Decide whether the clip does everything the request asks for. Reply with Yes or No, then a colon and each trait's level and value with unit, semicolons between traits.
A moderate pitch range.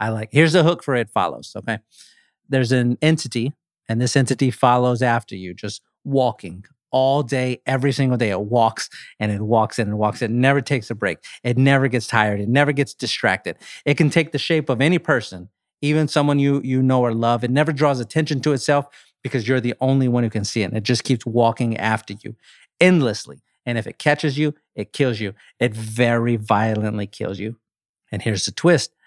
Yes: average, 4.1 semitones